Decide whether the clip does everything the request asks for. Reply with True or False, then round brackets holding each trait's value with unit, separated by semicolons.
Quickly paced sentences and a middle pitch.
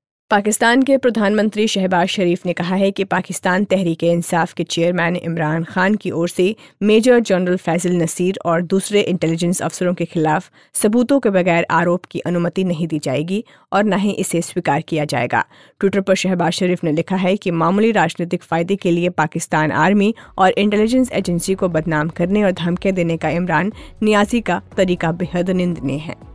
False (175 wpm; 180 Hz)